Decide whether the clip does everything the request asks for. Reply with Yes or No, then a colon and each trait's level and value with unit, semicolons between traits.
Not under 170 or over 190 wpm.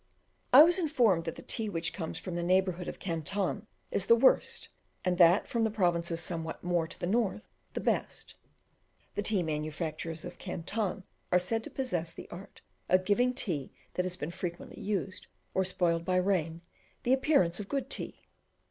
Yes: average, 180 wpm